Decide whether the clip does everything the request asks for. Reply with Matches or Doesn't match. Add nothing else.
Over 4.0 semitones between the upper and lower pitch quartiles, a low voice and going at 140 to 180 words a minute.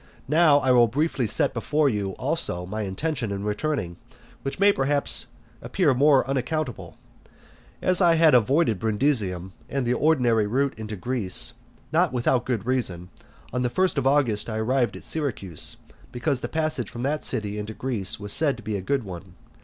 Matches